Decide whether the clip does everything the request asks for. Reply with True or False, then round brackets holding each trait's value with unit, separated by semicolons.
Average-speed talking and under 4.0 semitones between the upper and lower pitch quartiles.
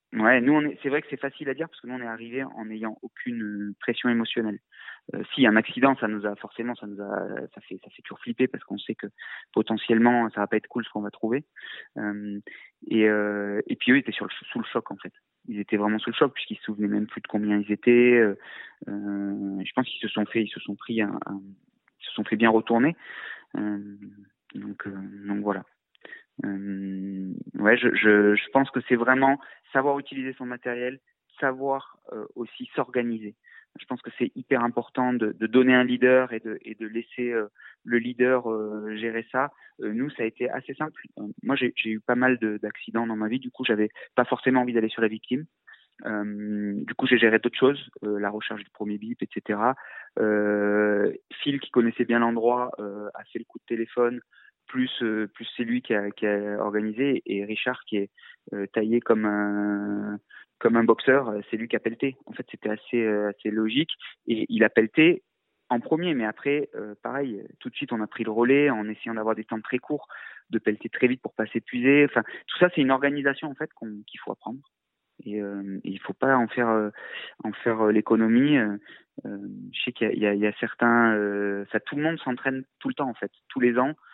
False (225 wpm; 3.2 semitones)